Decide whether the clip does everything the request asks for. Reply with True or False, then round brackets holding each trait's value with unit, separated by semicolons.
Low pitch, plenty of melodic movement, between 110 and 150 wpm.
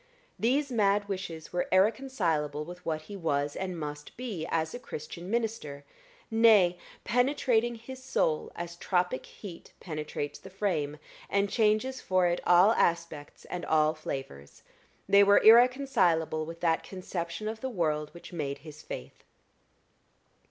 False (180 Hz; 5.7 semitones; 140 wpm)